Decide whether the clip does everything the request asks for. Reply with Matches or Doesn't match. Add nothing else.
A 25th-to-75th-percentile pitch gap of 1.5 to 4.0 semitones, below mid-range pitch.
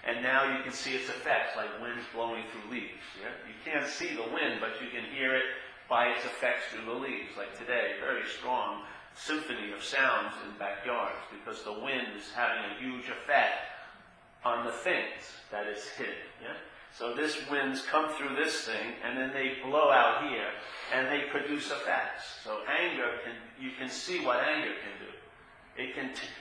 Matches